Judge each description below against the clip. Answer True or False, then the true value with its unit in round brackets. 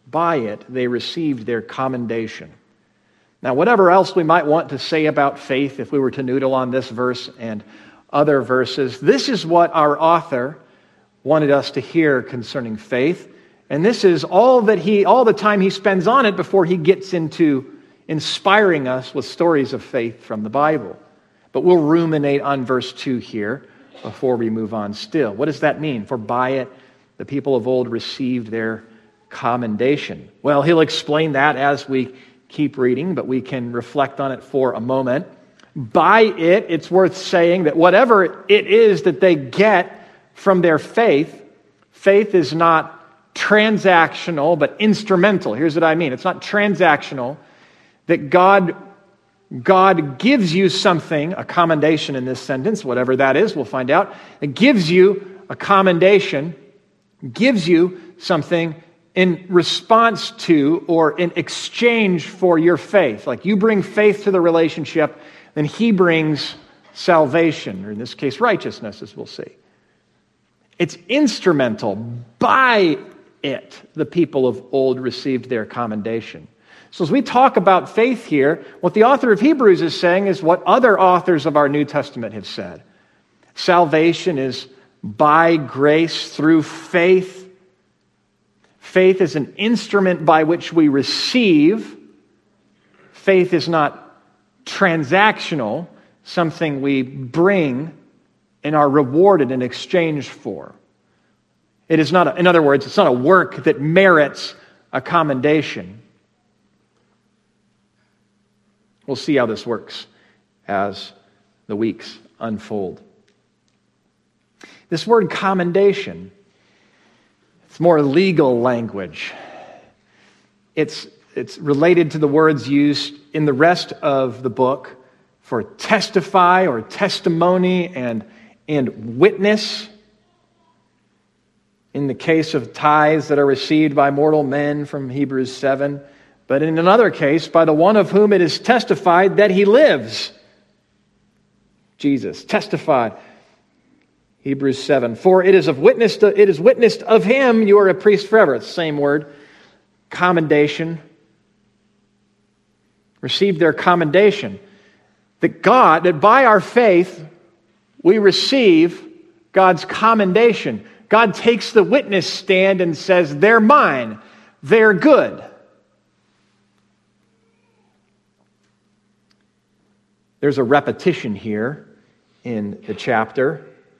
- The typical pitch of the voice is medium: True (165 Hz)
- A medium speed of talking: False (130 wpm)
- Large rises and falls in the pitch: True (6.0 semitones)